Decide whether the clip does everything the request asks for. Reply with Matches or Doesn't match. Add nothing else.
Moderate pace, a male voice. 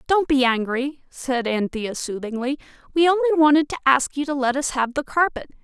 Doesn't match